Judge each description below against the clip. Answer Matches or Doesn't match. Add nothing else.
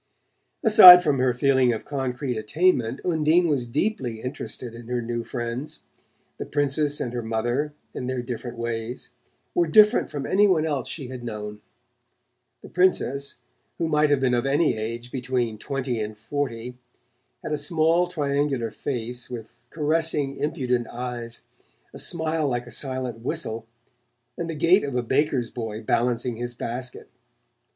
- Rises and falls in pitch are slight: Doesn't match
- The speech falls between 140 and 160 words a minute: Matches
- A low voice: Matches